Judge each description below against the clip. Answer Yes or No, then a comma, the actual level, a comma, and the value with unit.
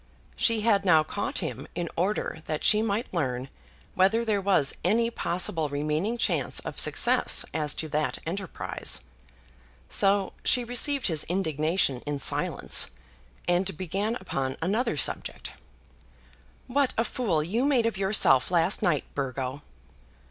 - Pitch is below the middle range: No, medium, 185 Hz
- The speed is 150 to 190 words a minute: No, slow, 135 wpm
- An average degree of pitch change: No, wide, 6.1 semitones